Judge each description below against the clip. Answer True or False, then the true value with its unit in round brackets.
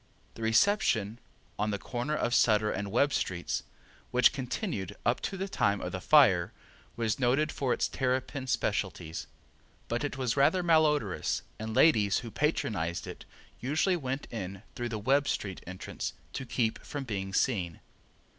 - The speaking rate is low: False (155 wpm)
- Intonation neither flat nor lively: False (5.7 semitones)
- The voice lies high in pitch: False (120 Hz)